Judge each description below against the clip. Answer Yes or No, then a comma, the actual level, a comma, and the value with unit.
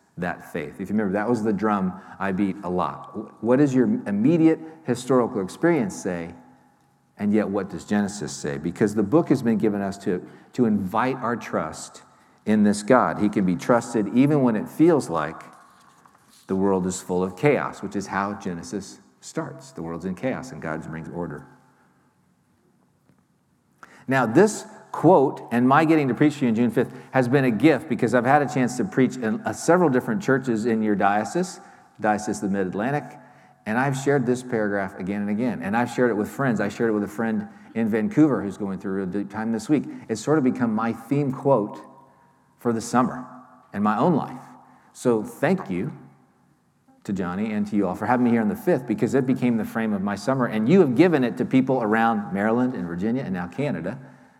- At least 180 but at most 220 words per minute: Yes, fast, 205 wpm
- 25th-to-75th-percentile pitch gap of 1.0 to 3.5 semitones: No, average, 4.7 semitones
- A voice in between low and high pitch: No, low, 115 Hz